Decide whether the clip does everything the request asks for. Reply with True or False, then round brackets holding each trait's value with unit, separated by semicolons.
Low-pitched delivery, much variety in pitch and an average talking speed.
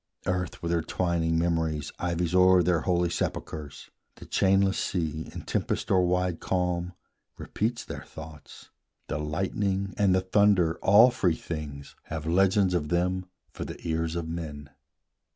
False (85 Hz; 2.4 semitones; 150 wpm)